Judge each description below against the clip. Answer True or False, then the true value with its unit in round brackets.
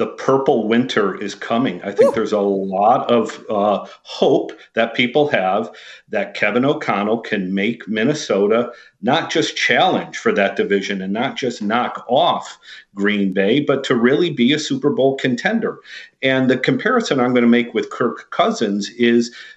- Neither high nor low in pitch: False (120 Hz)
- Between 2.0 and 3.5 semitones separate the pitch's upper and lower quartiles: False (4.6 semitones)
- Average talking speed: True (165 wpm)